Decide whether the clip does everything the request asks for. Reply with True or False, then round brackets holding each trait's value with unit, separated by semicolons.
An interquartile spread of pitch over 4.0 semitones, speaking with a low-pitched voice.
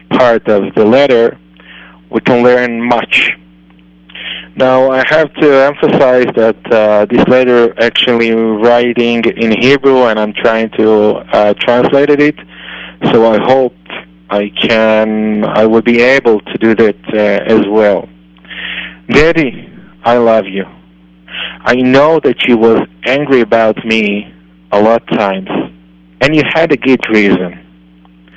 True (4.6 semitones; 110 Hz)